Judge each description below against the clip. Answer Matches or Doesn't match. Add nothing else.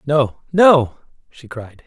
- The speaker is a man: Matches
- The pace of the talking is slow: Matches